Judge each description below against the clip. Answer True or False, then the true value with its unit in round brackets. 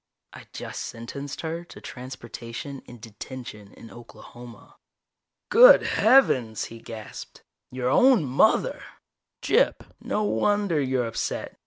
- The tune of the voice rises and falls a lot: True (6.3 semitones)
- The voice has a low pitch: True (130 Hz)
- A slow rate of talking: True (115 wpm)